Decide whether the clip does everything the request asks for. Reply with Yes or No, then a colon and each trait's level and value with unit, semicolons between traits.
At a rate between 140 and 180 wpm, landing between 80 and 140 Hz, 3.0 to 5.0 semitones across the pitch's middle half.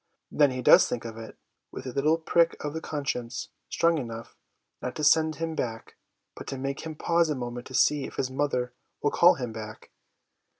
No: fast, 205 wpm; low, 135 Hz; average, 4.3 semitones